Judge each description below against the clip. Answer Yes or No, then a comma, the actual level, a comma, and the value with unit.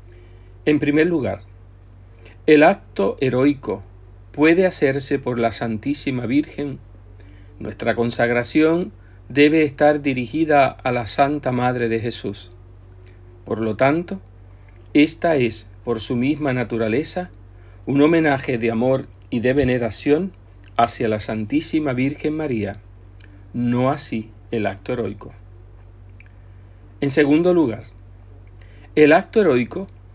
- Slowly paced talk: Yes, slow, 110 wpm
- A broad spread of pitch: Yes, wide, 6.6 semitones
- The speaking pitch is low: Yes, low, 115 Hz